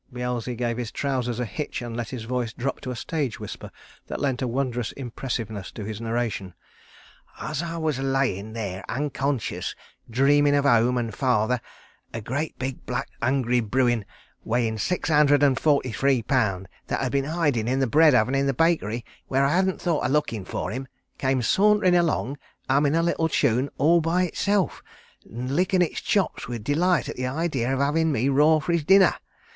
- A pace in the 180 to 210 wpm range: Yes, average, 190 wpm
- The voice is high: No, low, 135 Hz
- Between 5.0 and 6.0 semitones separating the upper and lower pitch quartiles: No, average, 4.0 semitones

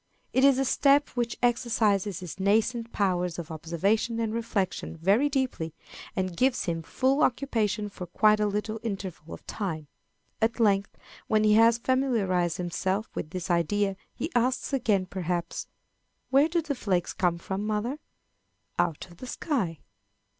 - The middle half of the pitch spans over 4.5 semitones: Yes, average, 4.9 semitones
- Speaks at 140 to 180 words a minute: Yes, average, 155 wpm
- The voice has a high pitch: Yes, high, 210 Hz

